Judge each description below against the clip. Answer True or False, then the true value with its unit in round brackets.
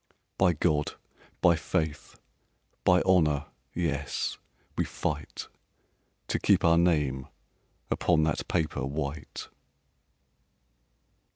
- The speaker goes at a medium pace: False (90 wpm)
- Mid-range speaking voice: False (80 Hz)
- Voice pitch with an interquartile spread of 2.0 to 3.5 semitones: True (2.8 semitones)